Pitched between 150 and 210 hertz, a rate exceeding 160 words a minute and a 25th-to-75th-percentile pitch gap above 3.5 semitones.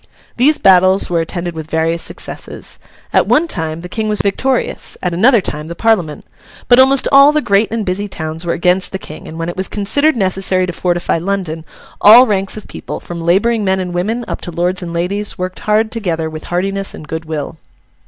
Yes: medium, 185 Hz; fast, 205 wpm; average, 4.0 semitones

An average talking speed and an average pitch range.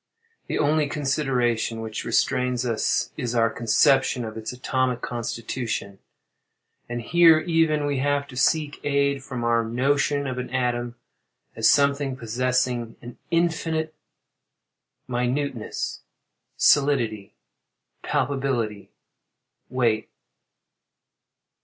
No: slow, 100 wpm; average, 3.3 semitones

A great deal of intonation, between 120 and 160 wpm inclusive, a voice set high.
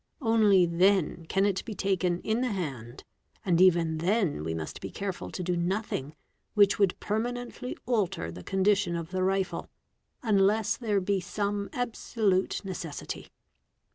No: average, 3.4 semitones; average, 145 wpm; high, 195 Hz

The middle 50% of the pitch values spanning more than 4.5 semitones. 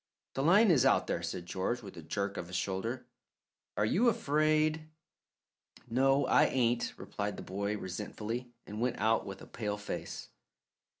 Yes: average, 5.3 semitones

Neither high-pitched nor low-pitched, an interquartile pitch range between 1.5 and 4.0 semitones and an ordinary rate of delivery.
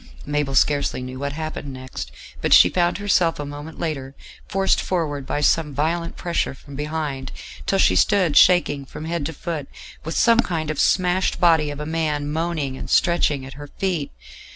Yes: medium, 155 Hz; average, 3.2 semitones; average, 180 wpm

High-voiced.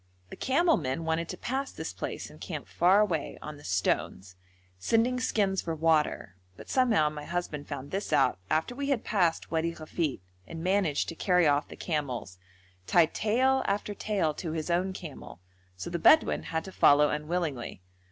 No: medium, 165 Hz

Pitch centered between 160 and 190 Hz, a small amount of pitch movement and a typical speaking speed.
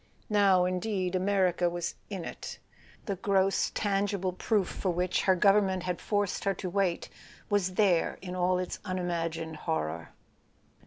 Yes: medium, 185 Hz; narrow, 2.0 semitones; average, 145 wpm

